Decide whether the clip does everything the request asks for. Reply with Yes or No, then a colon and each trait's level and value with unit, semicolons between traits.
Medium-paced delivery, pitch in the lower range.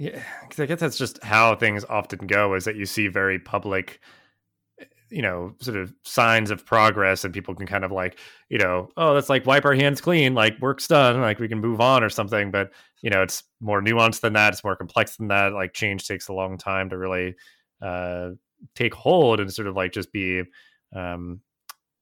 No: fast, 215 wpm; low, 100 Hz